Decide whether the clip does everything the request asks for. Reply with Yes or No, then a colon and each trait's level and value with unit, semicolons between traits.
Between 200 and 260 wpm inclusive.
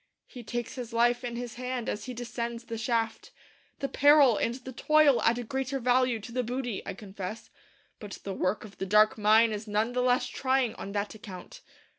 Yes: fast, 205 wpm